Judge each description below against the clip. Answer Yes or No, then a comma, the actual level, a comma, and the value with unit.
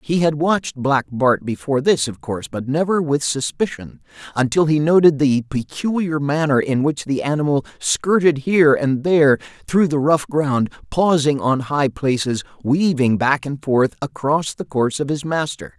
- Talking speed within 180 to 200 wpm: No, average, 170 wpm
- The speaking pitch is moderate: Yes, medium, 145 Hz